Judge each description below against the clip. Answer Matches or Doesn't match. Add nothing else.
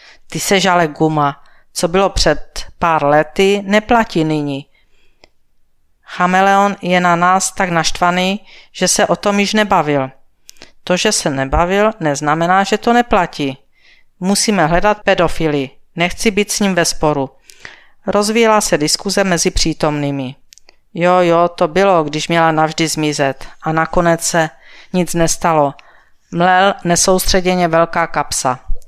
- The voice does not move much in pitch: Doesn't match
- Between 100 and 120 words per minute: Doesn't match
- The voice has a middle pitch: Matches